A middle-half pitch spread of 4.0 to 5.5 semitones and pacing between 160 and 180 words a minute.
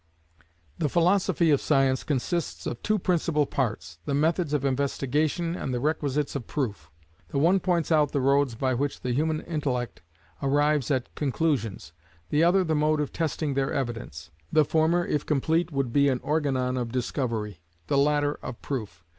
No: average, 3.6 semitones; average, 170 wpm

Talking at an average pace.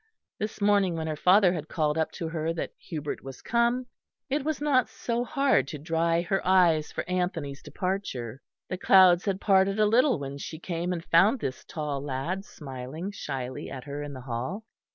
Yes: average, 190 wpm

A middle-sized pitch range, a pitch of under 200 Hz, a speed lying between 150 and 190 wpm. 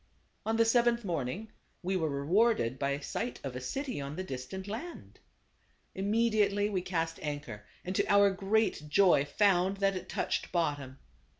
No: wide, 6.4 semitones; medium, 185 Hz; average, 170 wpm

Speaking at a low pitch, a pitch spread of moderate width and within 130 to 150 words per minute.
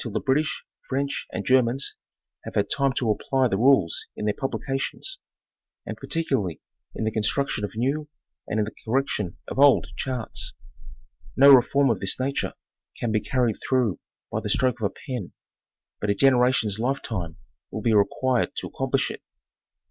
No: low, 125 Hz; average, 4.1 semitones; average, 165 wpm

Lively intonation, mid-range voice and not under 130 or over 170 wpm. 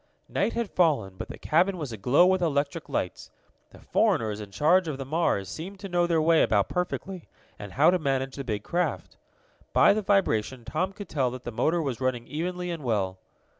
No: wide, 6.8 semitones; medium, 150 Hz; fast, 205 wpm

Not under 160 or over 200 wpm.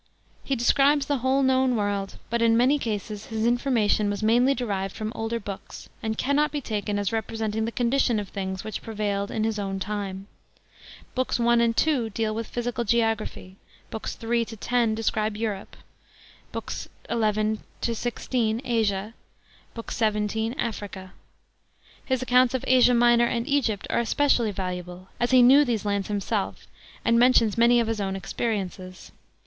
Yes: average, 165 wpm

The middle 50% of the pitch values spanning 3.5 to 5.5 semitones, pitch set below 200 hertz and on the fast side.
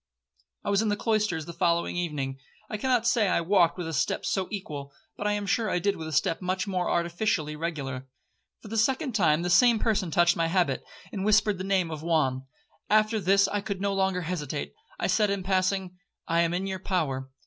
Yes: average, 3.8 semitones; medium, 185 Hz; fast, 215 wpm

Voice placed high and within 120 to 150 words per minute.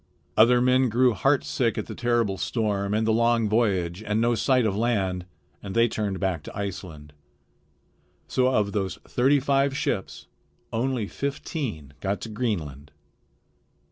No: low, 110 Hz; average, 145 wpm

